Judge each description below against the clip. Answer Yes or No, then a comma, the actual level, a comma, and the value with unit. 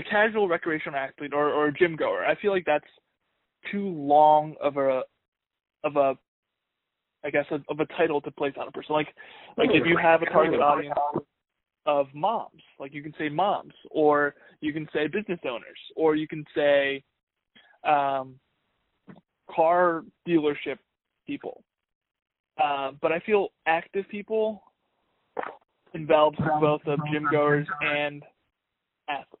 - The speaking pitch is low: No, medium, 150 Hz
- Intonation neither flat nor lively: No, narrow, 2.3 semitones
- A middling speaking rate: Yes, average, 145 wpm